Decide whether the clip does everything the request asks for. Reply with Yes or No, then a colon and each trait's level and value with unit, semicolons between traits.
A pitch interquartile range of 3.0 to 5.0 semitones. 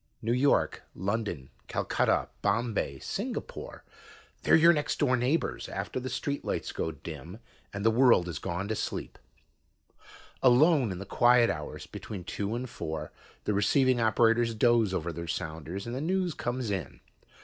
No: wide, 5.6 semitones